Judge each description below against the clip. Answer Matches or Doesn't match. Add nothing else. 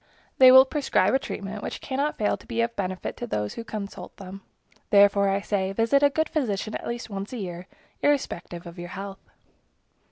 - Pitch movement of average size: Matches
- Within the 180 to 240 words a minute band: Matches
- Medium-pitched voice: Doesn't match